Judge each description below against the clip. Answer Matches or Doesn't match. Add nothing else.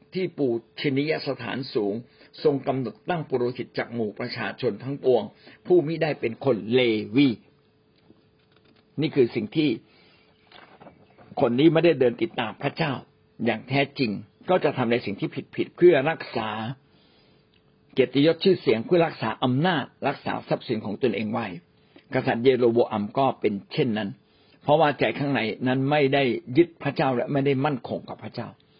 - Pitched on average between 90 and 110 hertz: Doesn't match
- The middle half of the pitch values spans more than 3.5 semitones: Matches